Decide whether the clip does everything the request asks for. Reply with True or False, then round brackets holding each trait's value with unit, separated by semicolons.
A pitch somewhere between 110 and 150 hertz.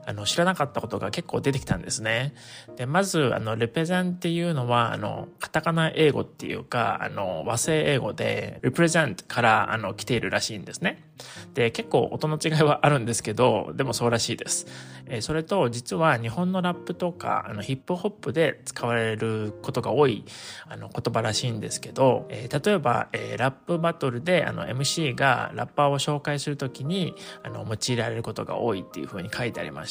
True (135 Hz)